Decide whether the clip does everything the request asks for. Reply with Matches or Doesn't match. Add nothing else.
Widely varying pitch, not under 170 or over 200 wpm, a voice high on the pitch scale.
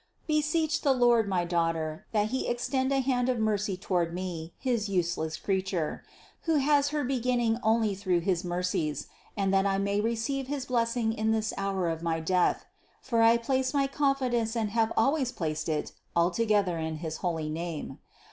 Matches